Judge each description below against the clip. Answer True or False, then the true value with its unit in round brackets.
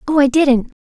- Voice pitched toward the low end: False (275 Hz)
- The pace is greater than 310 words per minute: False (215 wpm)